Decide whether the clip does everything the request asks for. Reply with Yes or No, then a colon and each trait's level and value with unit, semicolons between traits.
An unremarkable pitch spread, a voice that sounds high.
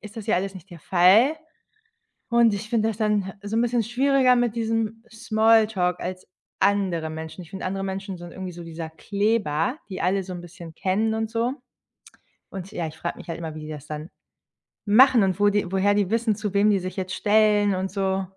Yes: average, 3.5 semitones; high, 200 Hz